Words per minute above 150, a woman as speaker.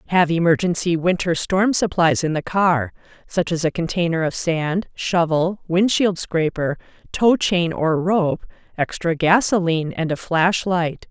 No: average, 140 wpm; female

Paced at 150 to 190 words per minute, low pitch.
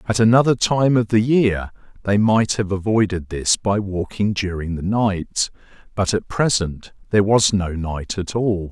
Yes: average, 170 wpm; low, 100 Hz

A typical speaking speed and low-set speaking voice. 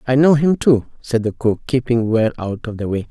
No: fast, 250 wpm; low, 120 Hz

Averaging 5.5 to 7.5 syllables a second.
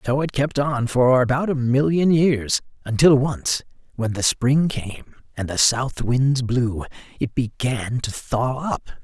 No: 3.7 syllables/s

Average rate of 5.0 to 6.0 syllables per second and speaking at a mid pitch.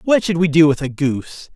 Yes: 5.6 syllables/s; medium, 160 Hz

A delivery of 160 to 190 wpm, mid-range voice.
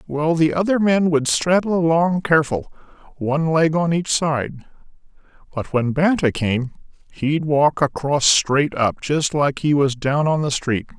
Yes: average, 165 wpm; medium, 150 Hz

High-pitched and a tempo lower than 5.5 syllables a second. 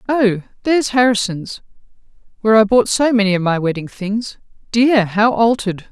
Yes: high, 215 Hz; 5.2 syllables/s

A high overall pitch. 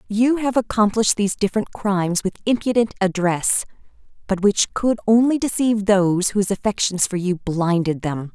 Yes: high, 205 Hz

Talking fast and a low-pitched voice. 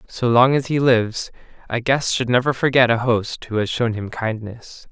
Yes: fast, 210 wpm; low, 120 Hz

